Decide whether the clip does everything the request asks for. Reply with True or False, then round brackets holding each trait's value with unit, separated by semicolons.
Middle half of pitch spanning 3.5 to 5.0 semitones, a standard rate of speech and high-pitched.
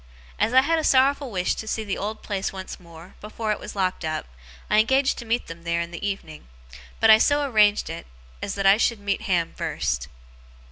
False (4.4 semitones; 220 wpm; 205 Hz)